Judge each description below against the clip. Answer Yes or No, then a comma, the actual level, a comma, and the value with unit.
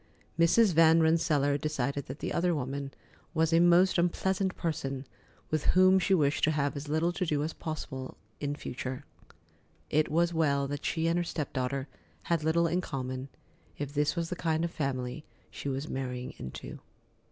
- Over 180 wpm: No, average, 175 wpm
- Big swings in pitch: No, average, 3.4 semitones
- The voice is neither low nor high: Yes, medium, 155 Hz